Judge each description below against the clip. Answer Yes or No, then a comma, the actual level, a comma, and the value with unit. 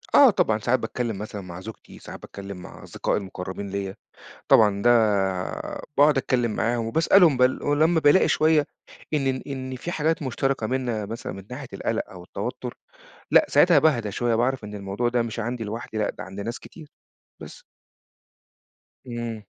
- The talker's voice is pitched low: Yes, low, 120 Hz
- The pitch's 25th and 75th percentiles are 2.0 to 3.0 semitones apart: No, average, 4.5 semitones